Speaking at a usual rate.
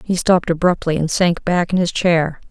No: fast, 215 wpm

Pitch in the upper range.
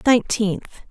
Yes: high, 220 Hz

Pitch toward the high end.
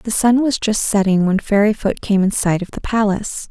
Yes: high, 205 Hz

